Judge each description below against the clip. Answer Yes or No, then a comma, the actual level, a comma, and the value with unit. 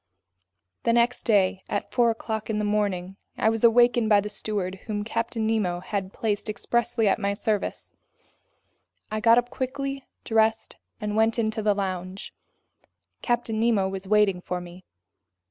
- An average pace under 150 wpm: No, average, 155 wpm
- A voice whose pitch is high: Yes, high, 215 Hz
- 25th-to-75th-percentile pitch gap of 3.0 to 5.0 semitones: No, narrow, 2.6 semitones